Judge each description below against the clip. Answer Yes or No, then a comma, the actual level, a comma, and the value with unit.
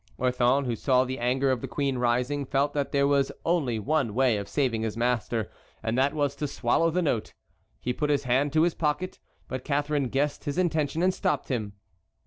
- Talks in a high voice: No, low, 135 Hz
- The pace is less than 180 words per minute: No, fast, 205 wpm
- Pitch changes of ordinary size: Yes, average, 3.1 semitones